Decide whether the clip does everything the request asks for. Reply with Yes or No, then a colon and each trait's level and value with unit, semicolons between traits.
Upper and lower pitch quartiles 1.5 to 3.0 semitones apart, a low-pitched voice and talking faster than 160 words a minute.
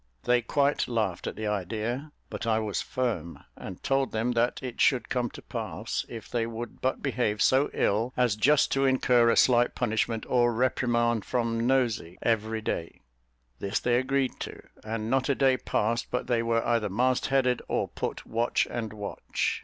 Yes: narrow, 2.4 semitones; low, 120 Hz; average, 180 wpm